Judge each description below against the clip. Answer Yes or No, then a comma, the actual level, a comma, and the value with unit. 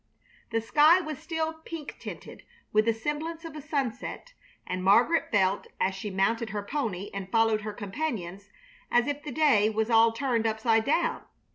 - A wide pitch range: Yes, wide, 6.3 semitones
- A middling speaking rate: Yes, average, 170 wpm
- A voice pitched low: No, high, 230 Hz